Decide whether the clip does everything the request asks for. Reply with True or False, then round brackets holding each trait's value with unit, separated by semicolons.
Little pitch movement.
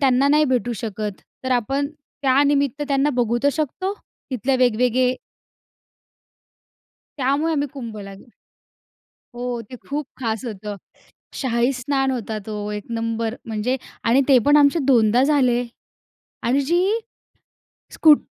False (3.5 semitones)